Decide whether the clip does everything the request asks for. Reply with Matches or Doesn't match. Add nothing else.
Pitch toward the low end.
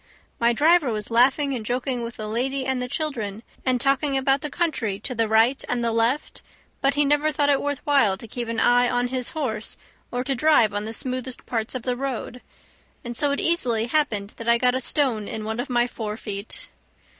Doesn't match